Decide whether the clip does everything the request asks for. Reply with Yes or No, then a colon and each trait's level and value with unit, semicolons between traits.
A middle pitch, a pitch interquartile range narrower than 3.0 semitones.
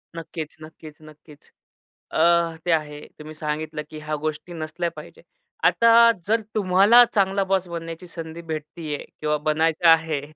Yes: medium, 160 Hz; narrow, 2.6 semitones